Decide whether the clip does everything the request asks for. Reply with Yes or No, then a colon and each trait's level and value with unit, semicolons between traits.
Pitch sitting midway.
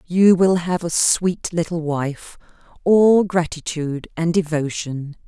Yes: medium, 170 Hz